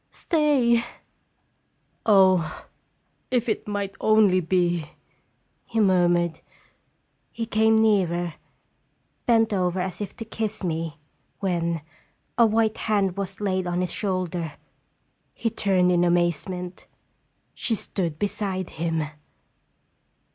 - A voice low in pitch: No, high, 190 Hz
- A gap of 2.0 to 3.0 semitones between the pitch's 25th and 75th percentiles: No, average, 3.7 semitones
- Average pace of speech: No, slow, 110 wpm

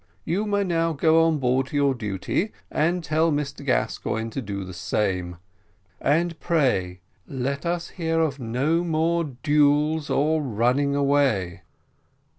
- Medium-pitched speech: Yes, medium, 145 Hz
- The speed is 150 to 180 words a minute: No, average, 140 wpm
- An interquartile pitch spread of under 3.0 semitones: No, average, 4.8 semitones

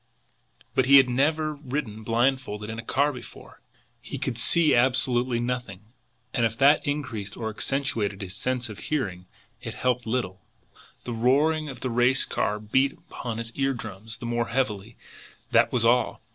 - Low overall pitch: Yes, low, 120 Hz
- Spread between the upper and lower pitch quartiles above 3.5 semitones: No, average, 3.1 semitones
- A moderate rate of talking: Yes, average, 160 wpm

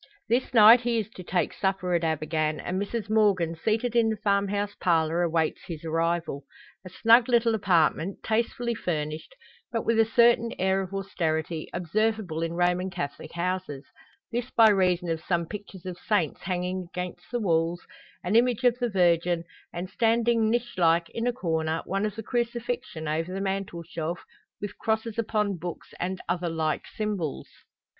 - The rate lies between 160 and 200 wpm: Yes, average, 165 wpm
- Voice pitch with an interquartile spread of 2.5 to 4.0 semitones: No, average, 4.7 semitones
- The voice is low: No, high, 190 Hz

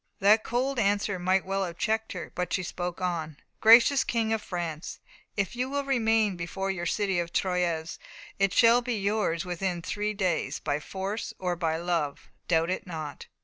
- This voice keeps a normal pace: Yes, average, 180 wpm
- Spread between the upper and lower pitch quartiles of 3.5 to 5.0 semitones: Yes, average, 4.0 semitones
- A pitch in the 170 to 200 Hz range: Yes, high, 190 Hz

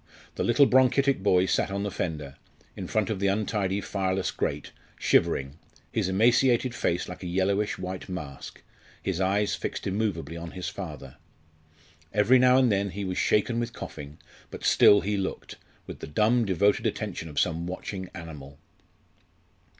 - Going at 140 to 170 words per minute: Yes, average, 160 wpm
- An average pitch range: Yes, average, 3.5 semitones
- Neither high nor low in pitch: No, very low, 95 Hz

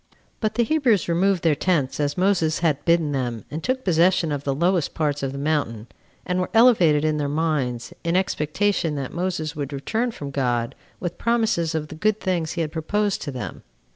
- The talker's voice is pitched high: No, medium, 160 Hz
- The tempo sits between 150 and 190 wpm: No, average, 200 wpm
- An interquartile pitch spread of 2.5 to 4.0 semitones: No, average, 4.4 semitones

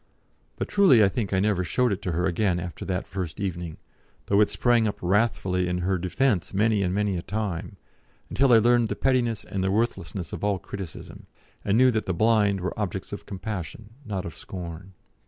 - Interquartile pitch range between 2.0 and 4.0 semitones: Yes, average, 3.3 semitones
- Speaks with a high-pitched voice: No, low, 100 Hz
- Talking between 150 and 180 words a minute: No, average, 200 wpm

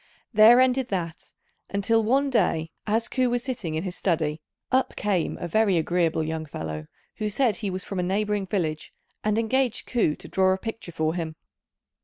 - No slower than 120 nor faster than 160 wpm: No, average, 185 wpm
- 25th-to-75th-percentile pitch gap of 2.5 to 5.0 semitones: No, wide, 5.6 semitones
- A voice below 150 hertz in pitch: No, high, 195 Hz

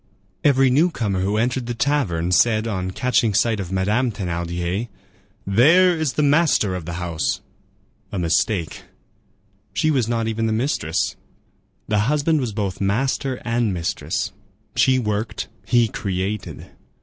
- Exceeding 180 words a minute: No, slow, 135 wpm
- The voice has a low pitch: Yes, low, 110 Hz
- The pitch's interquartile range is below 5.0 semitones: No, wide, 5.4 semitones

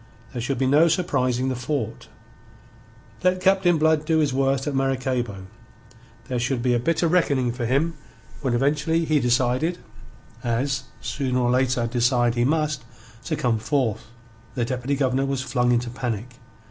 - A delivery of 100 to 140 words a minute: No, average, 160 wpm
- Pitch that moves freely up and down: No, average, 3.2 semitones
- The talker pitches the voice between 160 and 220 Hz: No, low, 130 Hz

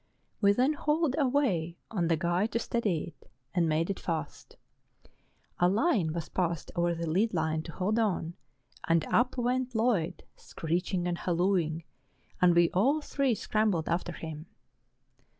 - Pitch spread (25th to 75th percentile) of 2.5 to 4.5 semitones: No, average, 5.3 semitones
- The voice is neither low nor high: Yes, medium, 180 Hz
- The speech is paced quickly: No, average, 155 wpm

